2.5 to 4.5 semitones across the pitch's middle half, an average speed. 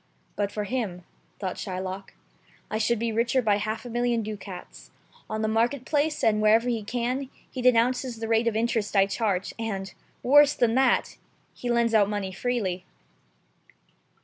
Yes: average, 2.9 semitones; average, 175 wpm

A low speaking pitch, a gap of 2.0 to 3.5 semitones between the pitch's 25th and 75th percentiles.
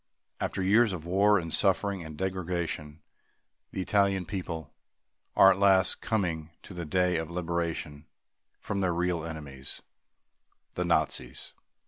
Yes: very low, 90 Hz; average, 2.9 semitones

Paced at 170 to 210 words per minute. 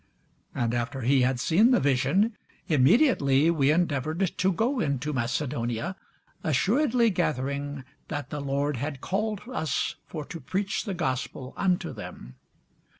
No: slow, 135 wpm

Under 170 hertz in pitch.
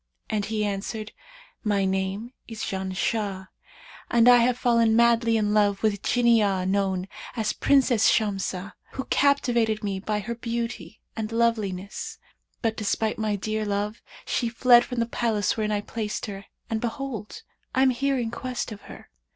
No: high, 220 Hz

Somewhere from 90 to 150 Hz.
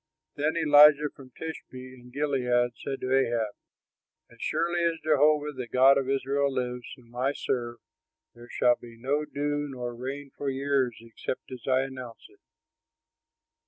Yes: low, 135 Hz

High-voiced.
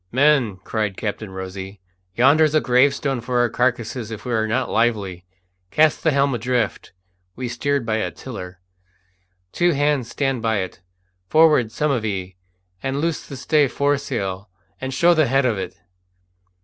No: low, 125 Hz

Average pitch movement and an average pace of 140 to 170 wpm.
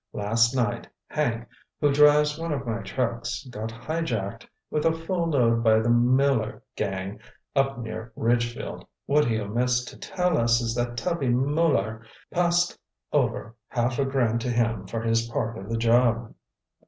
Yes: average, 3.4 semitones; average, 160 wpm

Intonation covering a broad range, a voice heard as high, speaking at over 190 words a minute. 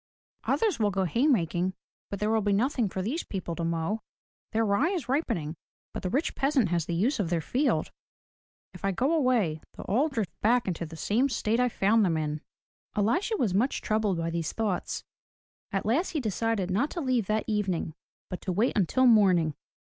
Yes: wide, 5.7 semitones; high, 210 Hz; average, 200 wpm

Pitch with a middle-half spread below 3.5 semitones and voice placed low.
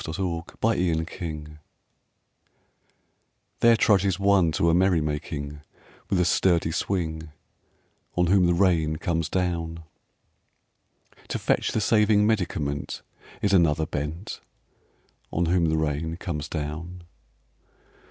Yes: average, 2.9 semitones; very low, 85 Hz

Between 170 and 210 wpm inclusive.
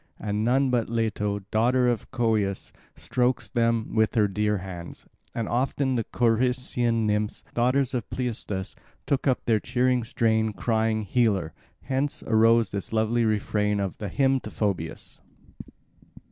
No: average, 140 wpm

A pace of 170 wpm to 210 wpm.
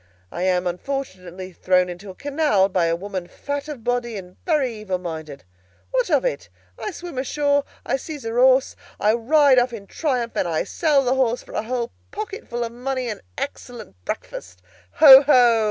Yes: average, 185 wpm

